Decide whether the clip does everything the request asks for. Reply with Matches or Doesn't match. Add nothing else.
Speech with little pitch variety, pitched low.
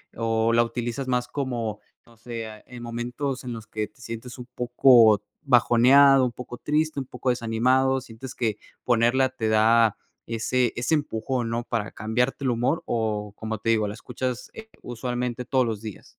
Matches